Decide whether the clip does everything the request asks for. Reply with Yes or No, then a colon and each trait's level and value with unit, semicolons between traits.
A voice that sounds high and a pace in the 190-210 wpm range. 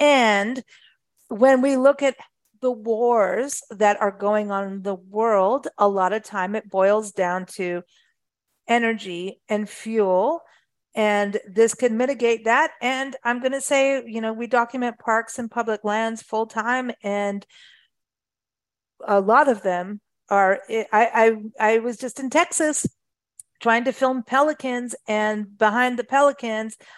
No: high, 225 Hz; average, 145 wpm